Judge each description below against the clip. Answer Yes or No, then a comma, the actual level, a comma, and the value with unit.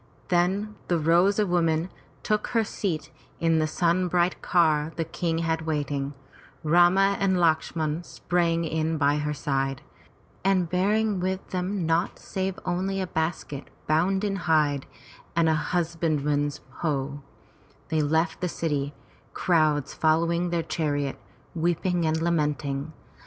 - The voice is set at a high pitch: No, medium, 165 Hz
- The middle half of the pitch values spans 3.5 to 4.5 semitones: No, narrow, 2.6 semitones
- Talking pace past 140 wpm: No, slow, 135 wpm